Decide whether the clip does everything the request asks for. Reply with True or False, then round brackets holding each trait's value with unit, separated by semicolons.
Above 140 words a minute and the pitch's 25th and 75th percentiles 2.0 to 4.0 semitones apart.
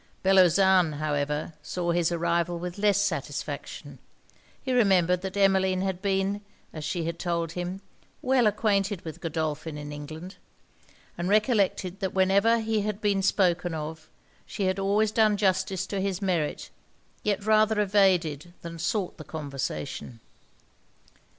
False (135 wpm; 3.2 semitones)